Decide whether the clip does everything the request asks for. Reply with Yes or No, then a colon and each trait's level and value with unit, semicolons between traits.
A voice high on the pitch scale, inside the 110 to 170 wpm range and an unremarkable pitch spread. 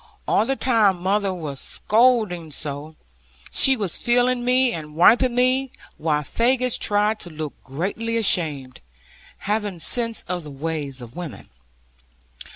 No: high, 195 Hz; slow, 135 wpm; wide, 7.5 semitones